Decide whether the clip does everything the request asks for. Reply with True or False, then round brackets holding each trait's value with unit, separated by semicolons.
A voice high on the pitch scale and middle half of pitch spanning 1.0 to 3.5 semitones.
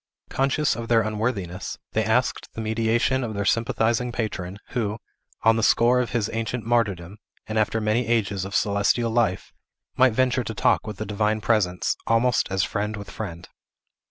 False (110 Hz; 2.4 semitones)